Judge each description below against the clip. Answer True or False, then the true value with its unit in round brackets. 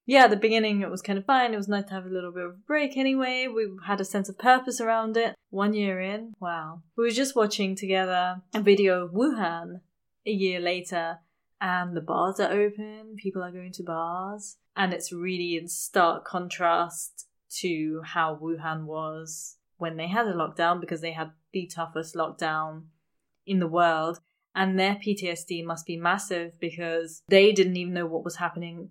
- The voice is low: False (180 Hz)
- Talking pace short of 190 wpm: False (195 wpm)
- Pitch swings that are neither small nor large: True (3.3 semitones)